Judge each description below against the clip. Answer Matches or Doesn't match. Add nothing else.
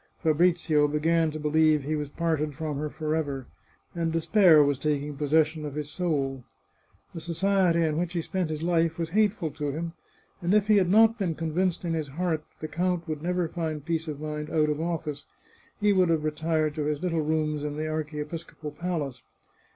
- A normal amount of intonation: Doesn't match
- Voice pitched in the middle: Matches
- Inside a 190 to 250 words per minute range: Matches